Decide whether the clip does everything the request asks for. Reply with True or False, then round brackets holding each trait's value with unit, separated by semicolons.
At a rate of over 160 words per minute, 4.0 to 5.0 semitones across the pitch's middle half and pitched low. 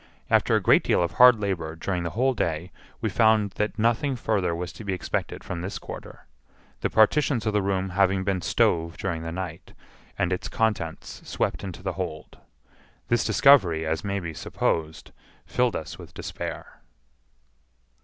True (170 wpm; 4.4 semitones; 95 Hz)